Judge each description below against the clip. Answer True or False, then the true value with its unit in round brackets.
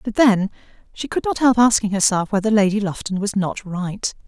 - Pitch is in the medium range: False (210 Hz)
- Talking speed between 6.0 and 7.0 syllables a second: False (5.2 syllables/s)